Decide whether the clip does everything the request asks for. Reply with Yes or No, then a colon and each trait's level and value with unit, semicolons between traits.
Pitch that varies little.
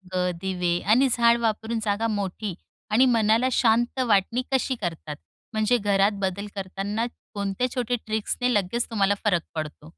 No: average, 3.3 semitones